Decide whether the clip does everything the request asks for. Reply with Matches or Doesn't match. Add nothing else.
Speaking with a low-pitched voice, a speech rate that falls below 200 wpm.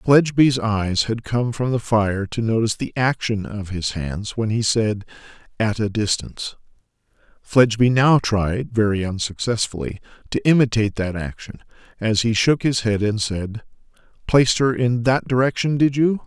Matches